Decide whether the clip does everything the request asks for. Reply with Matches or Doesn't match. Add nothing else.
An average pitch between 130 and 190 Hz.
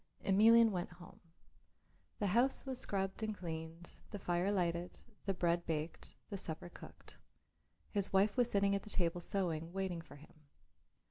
Matches